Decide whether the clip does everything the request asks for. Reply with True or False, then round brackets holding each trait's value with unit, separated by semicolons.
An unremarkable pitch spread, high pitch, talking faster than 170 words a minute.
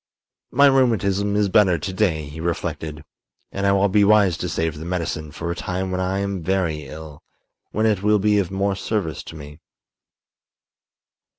False (4.0 semitones; 95 Hz; 180 wpm)